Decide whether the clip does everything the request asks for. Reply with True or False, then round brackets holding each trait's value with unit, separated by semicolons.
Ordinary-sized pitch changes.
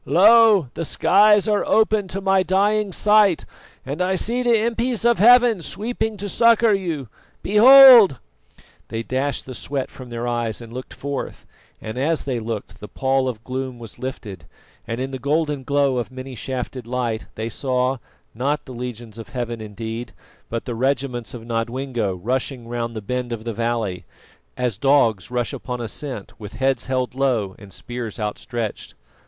False (7.6 semitones)